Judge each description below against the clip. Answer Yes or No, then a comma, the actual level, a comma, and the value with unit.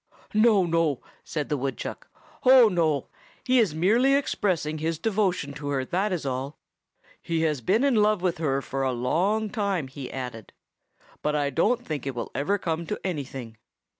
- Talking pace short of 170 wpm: No, average, 175 wpm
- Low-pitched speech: No, medium, 165 Hz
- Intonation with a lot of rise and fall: Yes, wide, 6.6 semitones